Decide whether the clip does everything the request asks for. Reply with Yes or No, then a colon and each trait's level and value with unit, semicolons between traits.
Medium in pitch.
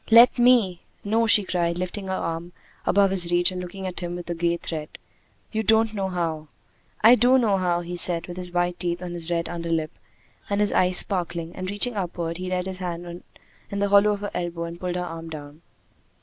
Yes: medium, 180 Hz